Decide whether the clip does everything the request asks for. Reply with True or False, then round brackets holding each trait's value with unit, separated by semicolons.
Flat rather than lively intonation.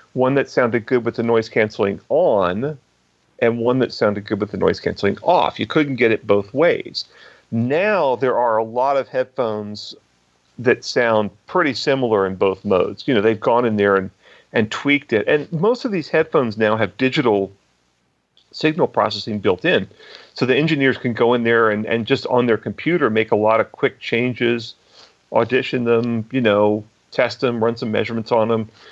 False (3.0 semitones)